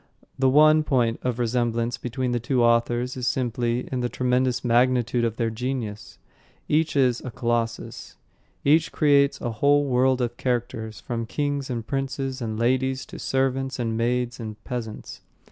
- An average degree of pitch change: No, narrow, 2.1 semitones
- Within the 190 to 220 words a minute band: No, average, 160 wpm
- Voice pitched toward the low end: Yes, low, 125 Hz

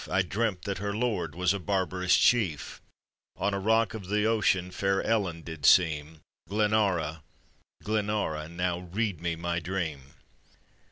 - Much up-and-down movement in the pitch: No, average, 3.7 semitones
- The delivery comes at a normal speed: Yes, average, 145 wpm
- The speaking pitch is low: Yes, very low, 95 Hz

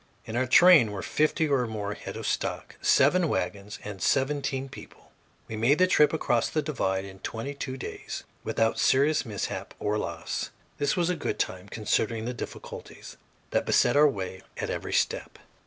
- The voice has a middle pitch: No, low, 120 Hz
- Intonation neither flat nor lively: No, wide, 5.7 semitones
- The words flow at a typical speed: Yes, average, 170 wpm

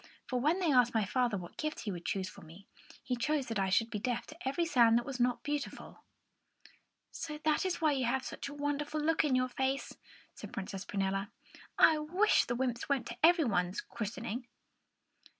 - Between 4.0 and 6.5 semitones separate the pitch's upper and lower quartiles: Yes, average, 5.0 semitones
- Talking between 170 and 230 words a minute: Yes, average, 200 wpm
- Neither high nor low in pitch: No, very high, 255 Hz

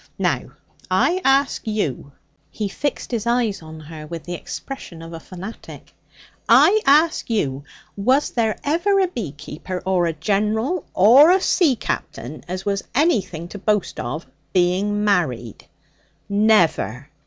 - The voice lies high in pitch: Yes, high, 200 Hz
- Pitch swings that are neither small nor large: No, wide, 7.2 semitones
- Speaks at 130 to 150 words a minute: Yes, average, 140 wpm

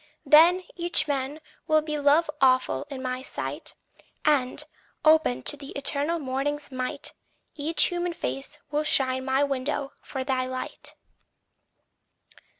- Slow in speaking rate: Yes, slow, 130 wpm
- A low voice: No, very high, 285 Hz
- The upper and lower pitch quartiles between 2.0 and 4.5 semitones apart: Yes, average, 2.8 semitones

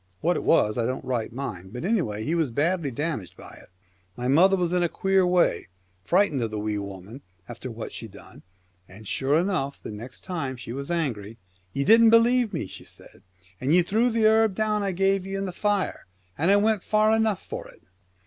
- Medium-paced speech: No, fast, 210 wpm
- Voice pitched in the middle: Yes, medium, 165 Hz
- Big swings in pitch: Yes, wide, 8.4 semitones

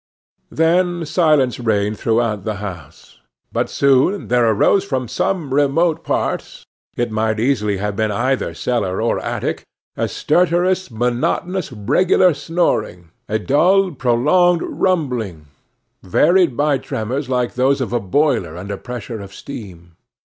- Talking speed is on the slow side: Yes, slow, 130 wpm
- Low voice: Yes, low, 125 Hz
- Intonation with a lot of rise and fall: Yes, wide, 7.0 semitones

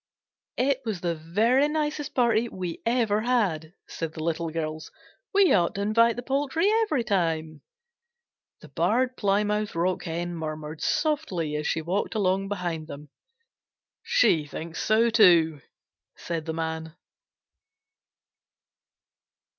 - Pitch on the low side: No, medium, 185 Hz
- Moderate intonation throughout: No, wide, 6.5 semitones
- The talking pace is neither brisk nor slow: No, slow, 125 wpm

